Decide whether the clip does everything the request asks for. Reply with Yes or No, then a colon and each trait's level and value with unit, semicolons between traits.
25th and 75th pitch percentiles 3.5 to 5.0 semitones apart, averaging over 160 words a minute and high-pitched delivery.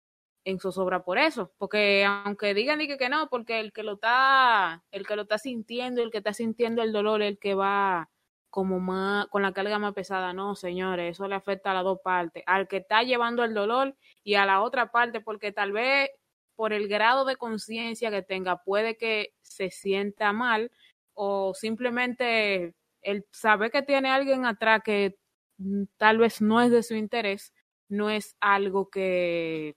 No: average, 3.0 semitones; average, 185 wpm; high, 210 Hz